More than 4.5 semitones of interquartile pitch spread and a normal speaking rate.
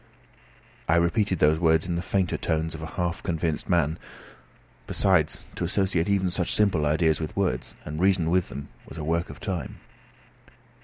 No: average, 2.8 semitones; average, 170 wpm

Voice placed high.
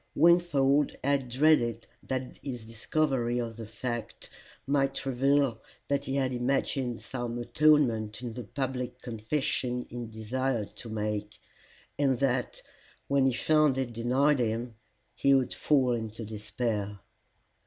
No: low, 125 Hz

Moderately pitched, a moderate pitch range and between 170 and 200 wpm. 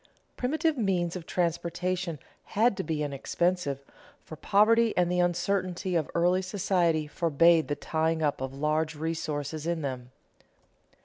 No: medium, 170 Hz; average, 3.1 semitones; slow, 135 wpm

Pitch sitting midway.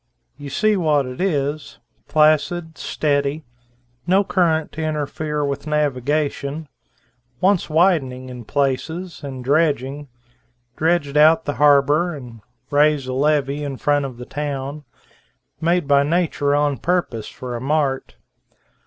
Yes: medium, 145 Hz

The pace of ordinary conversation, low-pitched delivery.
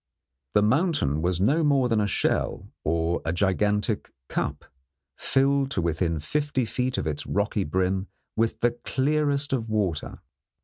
Yes: average, 145 wpm; low, 110 Hz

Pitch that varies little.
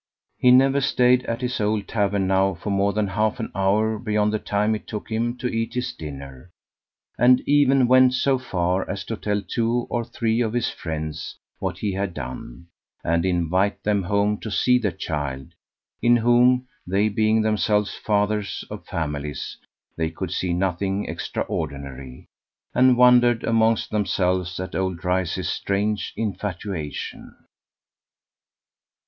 No: average, 4.1 semitones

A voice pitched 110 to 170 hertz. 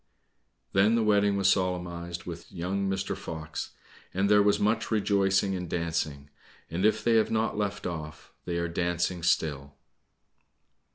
No: very low, 90 Hz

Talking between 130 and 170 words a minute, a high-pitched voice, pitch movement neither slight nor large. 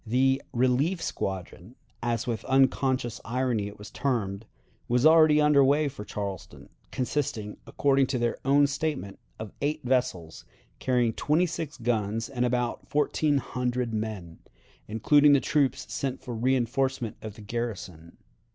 No: average, 140 wpm; low, 125 Hz; average, 4.0 semitones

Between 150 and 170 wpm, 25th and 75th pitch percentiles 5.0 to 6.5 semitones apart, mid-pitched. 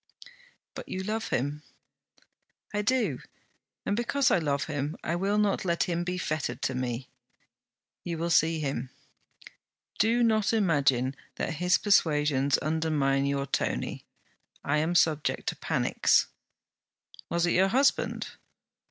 No: slow, 135 wpm; wide, 5.6 semitones; medium, 160 Hz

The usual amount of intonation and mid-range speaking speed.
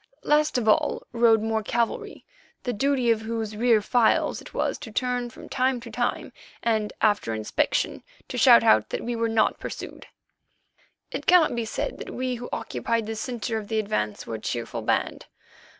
No: narrow, 2.3 semitones; average, 180 wpm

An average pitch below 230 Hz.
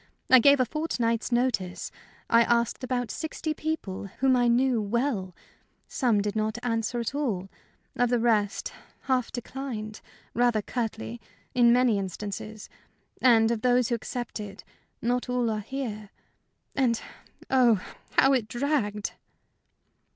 No: high, 235 Hz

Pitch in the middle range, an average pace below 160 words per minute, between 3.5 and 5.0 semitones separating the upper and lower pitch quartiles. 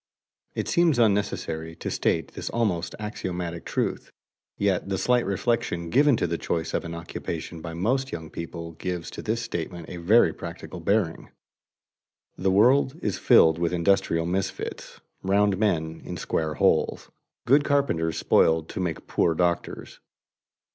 No: very low, 90 Hz; average, 150 wpm; average, 4.3 semitones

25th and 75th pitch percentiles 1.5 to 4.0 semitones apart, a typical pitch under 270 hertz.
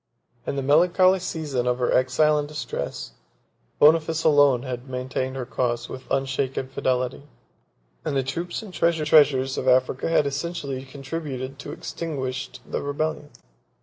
Yes: average, 3.1 semitones; medium, 140 Hz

